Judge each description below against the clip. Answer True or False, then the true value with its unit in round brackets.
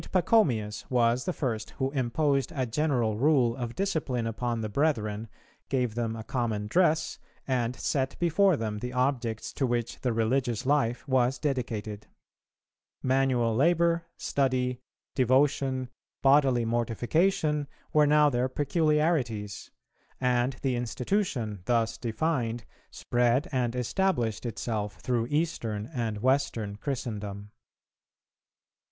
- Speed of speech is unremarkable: False (115 wpm)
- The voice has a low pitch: True (125 Hz)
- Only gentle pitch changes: False (3.8 semitones)